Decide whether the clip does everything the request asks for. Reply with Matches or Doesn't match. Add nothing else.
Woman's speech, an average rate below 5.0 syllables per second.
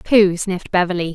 Doesn't match